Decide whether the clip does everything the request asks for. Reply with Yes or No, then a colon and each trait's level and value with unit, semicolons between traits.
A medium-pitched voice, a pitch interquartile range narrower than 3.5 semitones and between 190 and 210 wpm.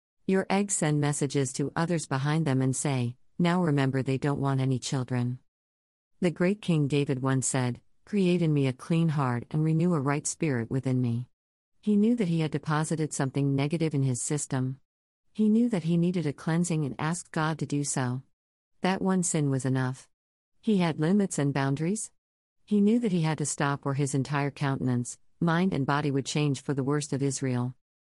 No: medium, 145 Hz; average, 4.0 semitones; average, 195 wpm